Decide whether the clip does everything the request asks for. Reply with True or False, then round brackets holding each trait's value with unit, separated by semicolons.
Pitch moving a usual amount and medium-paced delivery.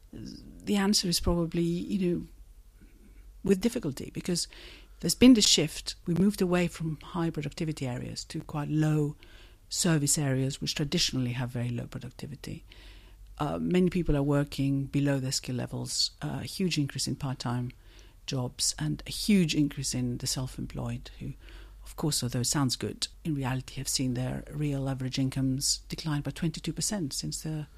True (4.4 semitones; 170 wpm)